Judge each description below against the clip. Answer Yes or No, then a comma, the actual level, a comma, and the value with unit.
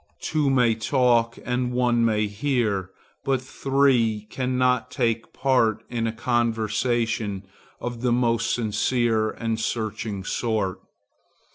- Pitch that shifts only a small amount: Yes, narrow, 2.3 semitones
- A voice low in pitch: Yes, low, 115 Hz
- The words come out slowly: Yes, slow, 115 wpm